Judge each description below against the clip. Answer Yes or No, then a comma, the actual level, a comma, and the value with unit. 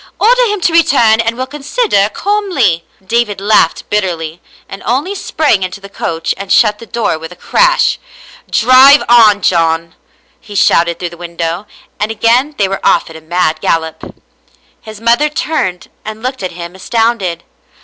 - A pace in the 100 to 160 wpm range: No, average, 170 wpm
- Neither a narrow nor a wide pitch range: No, wide, 6.7 semitones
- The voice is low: No, high, 210 Hz